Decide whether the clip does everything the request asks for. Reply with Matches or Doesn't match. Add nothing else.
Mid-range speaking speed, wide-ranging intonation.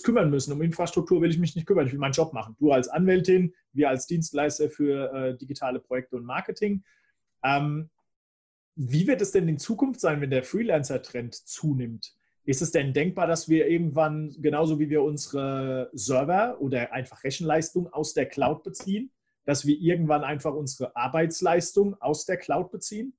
Doesn't match